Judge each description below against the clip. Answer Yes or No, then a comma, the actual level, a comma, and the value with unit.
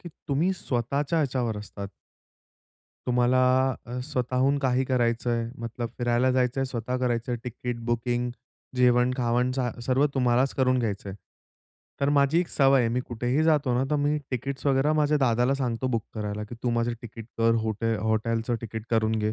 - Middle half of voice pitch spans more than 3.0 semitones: No, narrow, 2.4 semitones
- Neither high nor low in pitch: No, low, 125 Hz